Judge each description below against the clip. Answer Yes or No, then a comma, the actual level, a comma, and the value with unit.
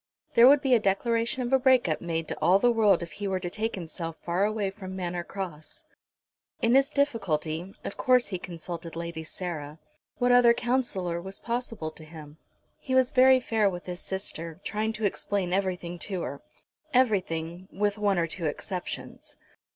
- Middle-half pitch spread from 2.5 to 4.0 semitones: No, average, 5.3 semitones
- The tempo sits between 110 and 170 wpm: No, average, 180 wpm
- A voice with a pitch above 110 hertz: Yes, high, 190 Hz